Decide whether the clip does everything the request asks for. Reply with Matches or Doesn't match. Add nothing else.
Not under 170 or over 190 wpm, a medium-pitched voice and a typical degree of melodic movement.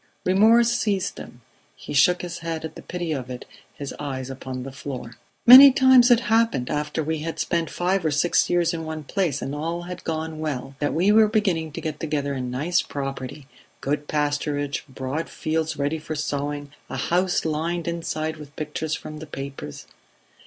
Matches